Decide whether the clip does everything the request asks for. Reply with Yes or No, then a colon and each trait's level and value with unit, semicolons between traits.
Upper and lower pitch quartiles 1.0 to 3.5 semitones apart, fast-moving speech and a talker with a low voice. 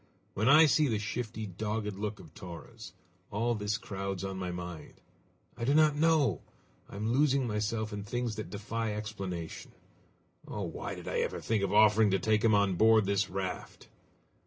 No: average, 2.7 semitones; average, 180 wpm; low, 105 Hz